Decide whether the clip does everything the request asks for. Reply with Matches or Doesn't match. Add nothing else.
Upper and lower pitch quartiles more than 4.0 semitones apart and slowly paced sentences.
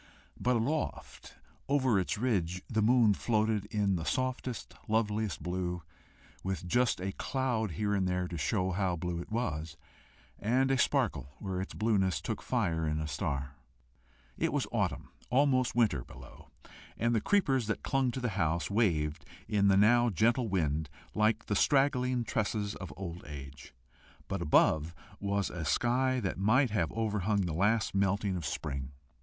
Doesn't match